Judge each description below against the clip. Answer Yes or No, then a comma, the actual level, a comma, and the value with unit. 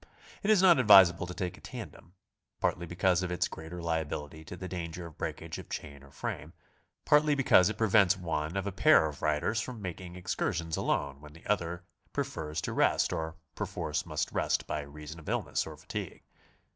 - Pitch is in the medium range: No, very low, 85 Hz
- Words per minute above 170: Yes, average, 200 wpm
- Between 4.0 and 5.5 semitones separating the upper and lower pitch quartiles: No, average, 3.5 semitones